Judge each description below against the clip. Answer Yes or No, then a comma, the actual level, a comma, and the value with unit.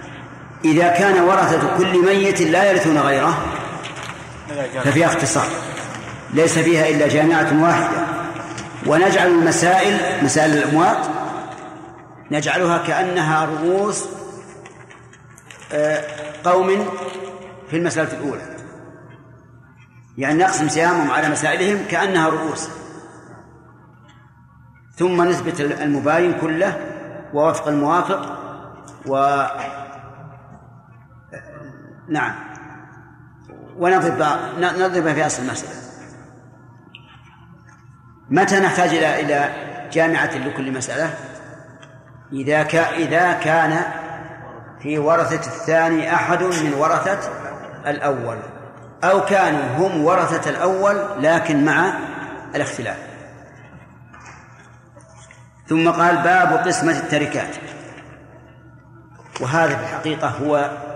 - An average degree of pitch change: Yes, average, 3.3 semitones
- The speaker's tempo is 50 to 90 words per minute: Yes, average, 80 wpm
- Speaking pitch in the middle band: Yes, medium, 160 Hz